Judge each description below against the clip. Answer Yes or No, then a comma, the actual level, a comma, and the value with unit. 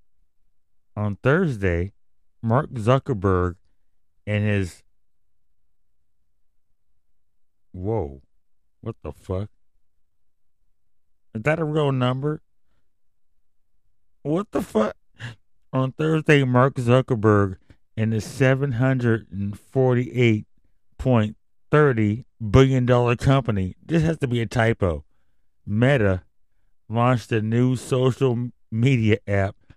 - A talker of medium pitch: No, low, 110 Hz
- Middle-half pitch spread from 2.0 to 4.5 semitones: No, wide, 5.6 semitones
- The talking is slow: Yes, slow, 95 wpm